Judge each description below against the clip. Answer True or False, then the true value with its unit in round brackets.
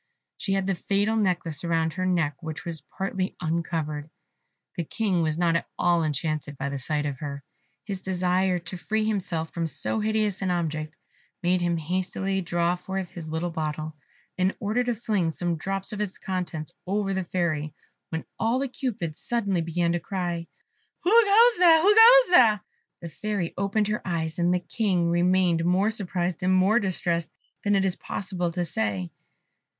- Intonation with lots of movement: False (3.3 semitones)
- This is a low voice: False (180 Hz)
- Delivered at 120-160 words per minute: False (175 wpm)